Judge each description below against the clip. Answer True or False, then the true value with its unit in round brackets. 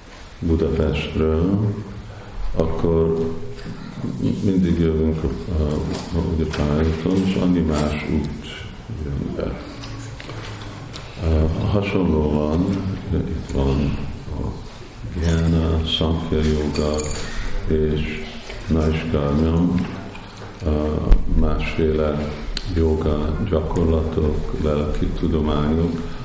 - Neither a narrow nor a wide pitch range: True (3.6 semitones)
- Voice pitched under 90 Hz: True (80 Hz)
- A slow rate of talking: True (60 wpm)